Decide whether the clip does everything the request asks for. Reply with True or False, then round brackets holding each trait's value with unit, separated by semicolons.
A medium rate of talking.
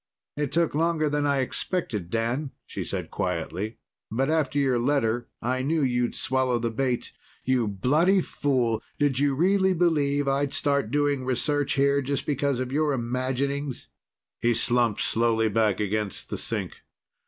True (155 wpm)